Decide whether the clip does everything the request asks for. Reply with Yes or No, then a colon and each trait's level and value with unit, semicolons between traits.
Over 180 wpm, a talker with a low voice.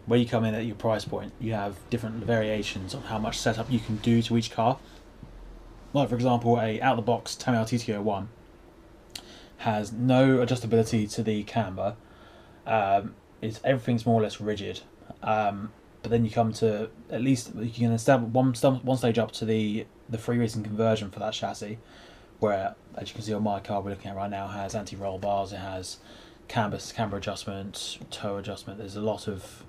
Yes: average, 200 wpm; low, 110 Hz